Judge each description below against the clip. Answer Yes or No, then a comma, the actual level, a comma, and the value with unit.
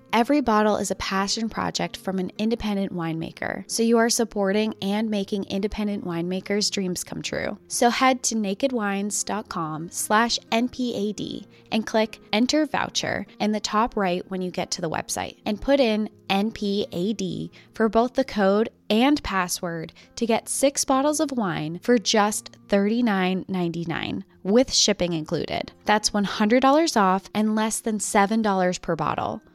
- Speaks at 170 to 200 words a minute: No, average, 140 wpm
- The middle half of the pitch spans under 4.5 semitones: Yes, average, 3.2 semitones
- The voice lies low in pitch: No, high, 210 Hz